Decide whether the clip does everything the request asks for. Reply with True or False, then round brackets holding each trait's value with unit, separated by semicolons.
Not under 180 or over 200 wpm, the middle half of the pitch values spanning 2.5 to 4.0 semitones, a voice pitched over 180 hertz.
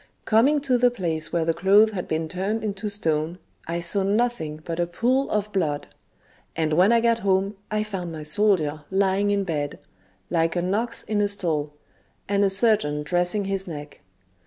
False (185 wpm; 4.5 semitones; 190 Hz)